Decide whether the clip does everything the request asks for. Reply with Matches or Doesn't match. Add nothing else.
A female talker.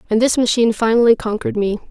Matches